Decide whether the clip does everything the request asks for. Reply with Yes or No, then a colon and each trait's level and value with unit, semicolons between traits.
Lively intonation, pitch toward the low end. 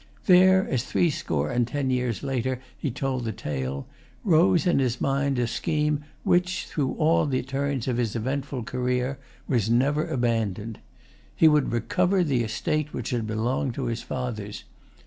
No: average, 4.0 semitones; low, 130 Hz